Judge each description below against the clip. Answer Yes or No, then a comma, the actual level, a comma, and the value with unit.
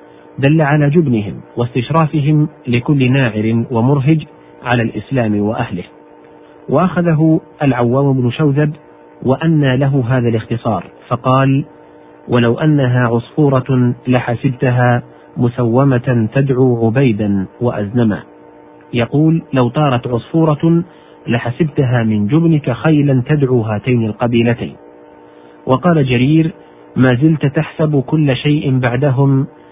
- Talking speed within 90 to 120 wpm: Yes, average, 95 wpm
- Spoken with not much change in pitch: No, average, 4.2 semitones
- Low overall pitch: Yes, low, 125 Hz